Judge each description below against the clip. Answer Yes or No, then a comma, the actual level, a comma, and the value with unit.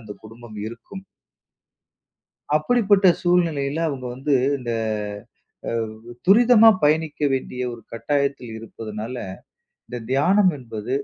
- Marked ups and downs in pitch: Yes, wide, 7.3 semitones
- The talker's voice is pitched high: No, medium, 140 Hz